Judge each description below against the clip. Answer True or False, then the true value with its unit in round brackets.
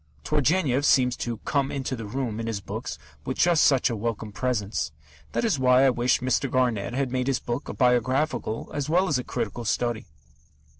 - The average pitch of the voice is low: True (125 Hz)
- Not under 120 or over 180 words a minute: False (195 wpm)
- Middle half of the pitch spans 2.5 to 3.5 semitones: True (2.8 semitones)